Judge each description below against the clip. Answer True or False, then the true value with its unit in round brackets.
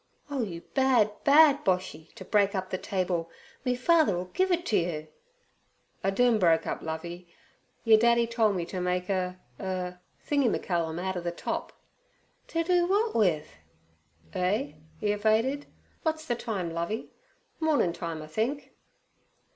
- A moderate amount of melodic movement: False (6.1 semitones)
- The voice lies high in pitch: True (200 Hz)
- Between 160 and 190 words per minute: False (145 wpm)